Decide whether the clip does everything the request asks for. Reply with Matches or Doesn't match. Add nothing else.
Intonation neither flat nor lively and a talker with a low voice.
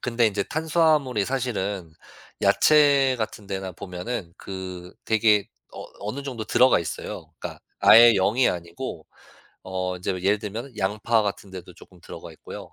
Matches